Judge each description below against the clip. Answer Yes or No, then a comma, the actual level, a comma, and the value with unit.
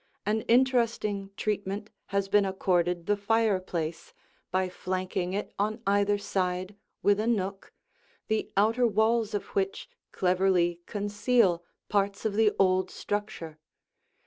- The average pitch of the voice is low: No, high, 200 Hz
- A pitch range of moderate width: No, narrow, 2.3 semitones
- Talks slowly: Yes, slow, 120 wpm